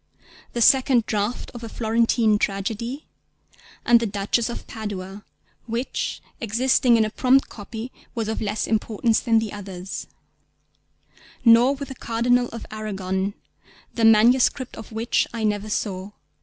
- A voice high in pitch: Yes, high, 225 Hz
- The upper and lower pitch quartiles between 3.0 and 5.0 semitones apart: No, narrow, 2.4 semitones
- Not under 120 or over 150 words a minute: Yes, average, 140 wpm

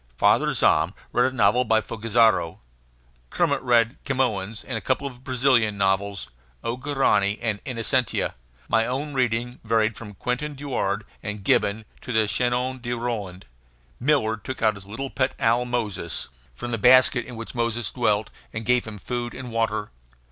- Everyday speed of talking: Yes, average, 160 wpm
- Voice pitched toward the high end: No, low, 115 Hz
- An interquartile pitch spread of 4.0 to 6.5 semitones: No, average, 2.9 semitones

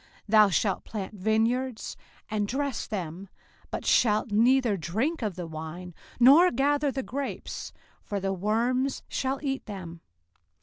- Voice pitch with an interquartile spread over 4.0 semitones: Yes, wide, 5.4 semitones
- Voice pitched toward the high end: Yes, high, 220 Hz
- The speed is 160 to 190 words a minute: No, average, 140 wpm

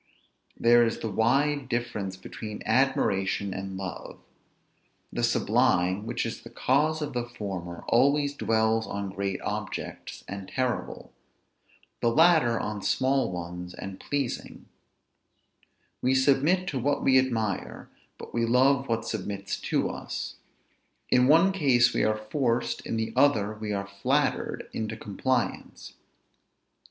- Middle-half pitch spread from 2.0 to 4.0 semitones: No, average, 4.7 semitones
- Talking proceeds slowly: Yes, slow, 130 wpm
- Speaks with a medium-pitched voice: No, low, 115 Hz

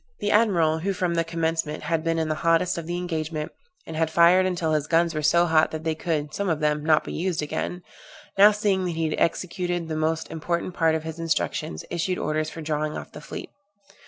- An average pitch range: No, narrow, 2.0 semitones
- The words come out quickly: Yes, fast, 225 wpm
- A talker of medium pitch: Yes, medium, 165 Hz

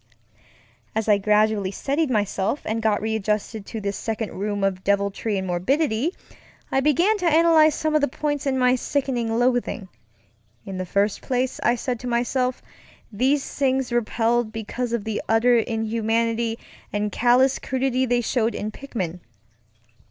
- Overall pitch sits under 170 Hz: No, high, 230 Hz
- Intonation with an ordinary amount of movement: Yes, average, 3.6 semitones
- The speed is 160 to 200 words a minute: No, average, 150 wpm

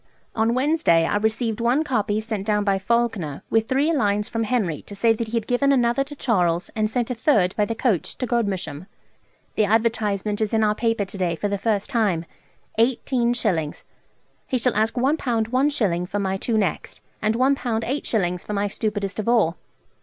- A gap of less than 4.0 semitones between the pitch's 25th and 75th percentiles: Yes, average, 3.1 semitones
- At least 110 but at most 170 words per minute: No, average, 190 wpm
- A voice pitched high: Yes, high, 220 Hz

